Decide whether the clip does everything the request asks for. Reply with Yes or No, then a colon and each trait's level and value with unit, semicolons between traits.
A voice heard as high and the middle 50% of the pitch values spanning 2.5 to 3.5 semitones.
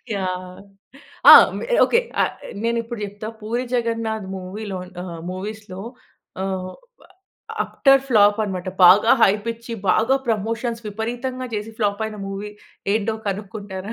Yes: high, 210 Hz; average, 2.9 semitones